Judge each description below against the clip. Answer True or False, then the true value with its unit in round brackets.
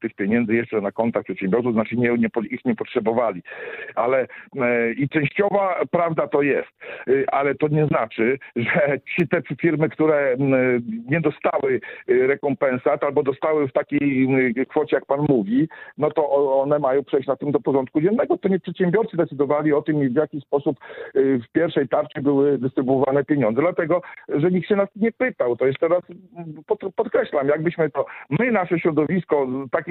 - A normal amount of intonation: True (4.3 semitones)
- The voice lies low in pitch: False (150 Hz)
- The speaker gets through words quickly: True (165 wpm)